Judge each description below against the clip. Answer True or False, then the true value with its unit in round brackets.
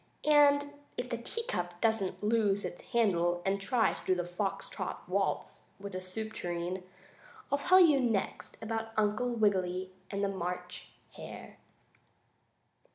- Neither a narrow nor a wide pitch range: True (4.3 semitones)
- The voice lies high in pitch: True (205 Hz)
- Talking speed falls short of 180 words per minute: True (140 wpm)